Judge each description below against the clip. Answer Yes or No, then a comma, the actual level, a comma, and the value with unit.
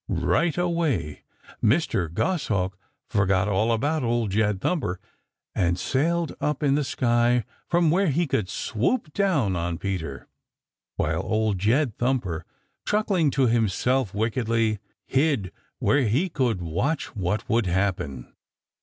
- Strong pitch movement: Yes, wide, 7.5 semitones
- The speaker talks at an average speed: No, slow, 130 wpm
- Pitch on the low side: Yes, low, 115 Hz